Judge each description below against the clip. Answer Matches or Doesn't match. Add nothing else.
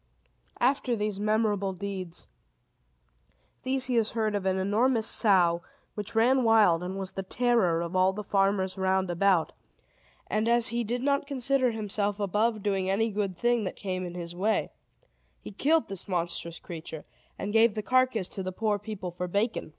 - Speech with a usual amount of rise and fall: Matches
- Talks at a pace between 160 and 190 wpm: Matches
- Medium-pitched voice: Doesn't match